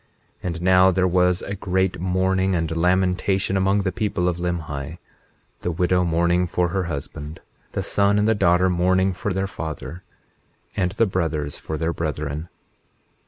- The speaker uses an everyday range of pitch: No, narrow, 2.1 semitones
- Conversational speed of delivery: Yes, average, 165 wpm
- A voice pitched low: Yes, very low, 90 Hz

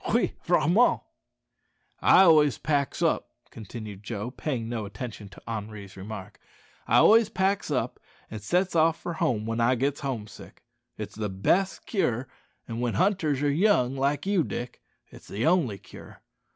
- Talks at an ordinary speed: Yes, average, 160 wpm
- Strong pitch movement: Yes, wide, 7.2 semitones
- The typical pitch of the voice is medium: No, low, 130 Hz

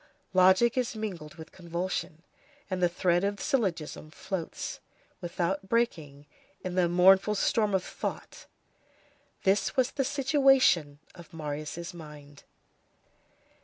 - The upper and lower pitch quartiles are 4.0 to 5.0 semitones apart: Yes, average, 4.4 semitones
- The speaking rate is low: Yes, slow, 120 wpm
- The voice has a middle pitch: Yes, medium, 180 Hz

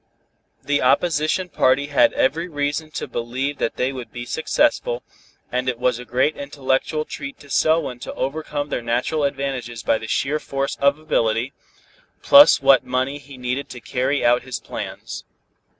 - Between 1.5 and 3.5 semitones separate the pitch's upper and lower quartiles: Yes, average, 2.7 semitones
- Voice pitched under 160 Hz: Yes, low, 135 Hz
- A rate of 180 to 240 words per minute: No, average, 165 wpm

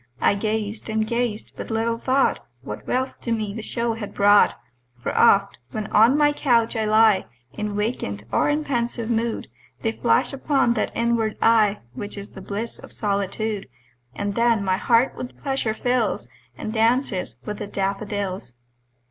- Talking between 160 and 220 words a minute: Yes, average, 165 wpm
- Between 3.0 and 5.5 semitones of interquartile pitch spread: No, narrow, 2.5 semitones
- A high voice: Yes, high, 220 Hz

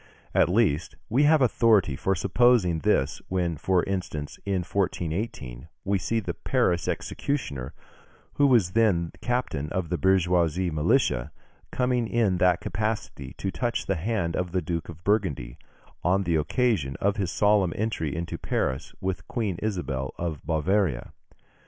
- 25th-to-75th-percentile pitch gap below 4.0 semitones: No, average, 4.9 semitones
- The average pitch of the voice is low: Yes, very low, 90 Hz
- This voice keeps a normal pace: Yes, average, 145 wpm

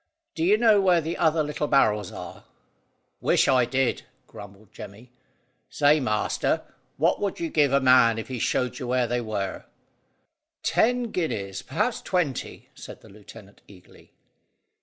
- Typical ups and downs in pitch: No, wide, 6.9 semitones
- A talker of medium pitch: No, low, 130 Hz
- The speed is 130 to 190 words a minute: Yes, average, 150 wpm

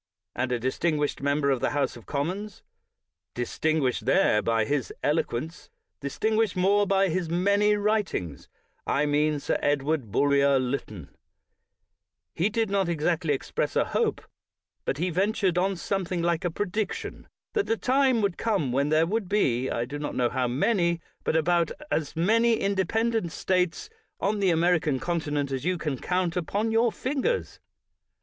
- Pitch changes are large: Yes, wide, 6.0 semitones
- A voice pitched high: No, medium, 170 Hz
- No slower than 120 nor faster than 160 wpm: No, average, 170 wpm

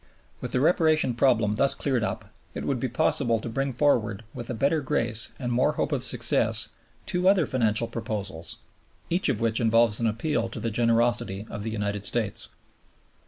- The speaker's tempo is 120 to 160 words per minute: No, average, 180 wpm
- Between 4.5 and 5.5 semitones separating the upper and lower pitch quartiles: No, average, 3.3 semitones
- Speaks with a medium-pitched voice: No, low, 115 Hz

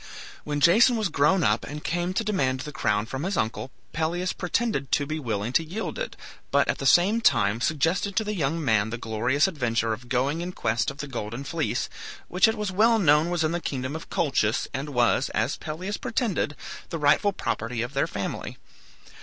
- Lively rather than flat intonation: Yes, wide, 6.6 semitones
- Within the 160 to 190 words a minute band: No, fast, 205 wpm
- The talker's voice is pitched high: No, medium, 150 Hz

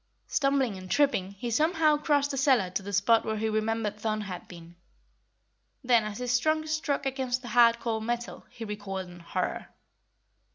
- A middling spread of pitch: Yes, average, 4.8 semitones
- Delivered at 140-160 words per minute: No, average, 170 wpm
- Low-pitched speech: No, high, 230 Hz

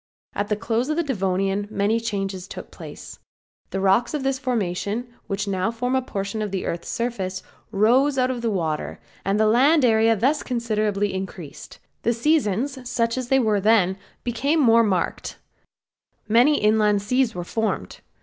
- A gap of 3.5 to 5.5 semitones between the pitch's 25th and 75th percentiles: Yes, average, 4.0 semitones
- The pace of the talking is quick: No, average, 165 wpm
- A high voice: Yes, high, 220 Hz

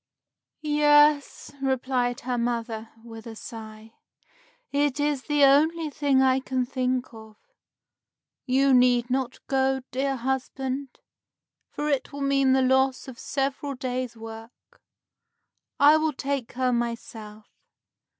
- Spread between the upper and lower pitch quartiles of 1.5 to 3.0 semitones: Yes, narrow, 2.5 semitones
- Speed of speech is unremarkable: No, slow, 120 wpm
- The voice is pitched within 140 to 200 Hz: No, very high, 260 Hz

